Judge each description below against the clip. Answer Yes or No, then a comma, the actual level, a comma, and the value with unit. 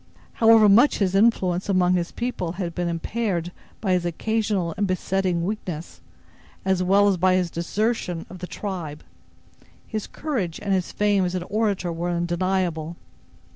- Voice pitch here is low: No, medium, 185 Hz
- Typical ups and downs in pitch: Yes, average, 3.0 semitones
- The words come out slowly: No, average, 155 wpm